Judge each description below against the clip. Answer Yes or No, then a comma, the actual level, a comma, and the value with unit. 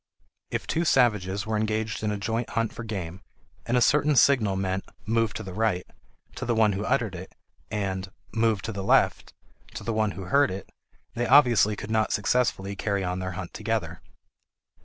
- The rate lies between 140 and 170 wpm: No, average, 190 wpm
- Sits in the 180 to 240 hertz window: No, low, 105 Hz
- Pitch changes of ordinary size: Yes, average, 3.0 semitones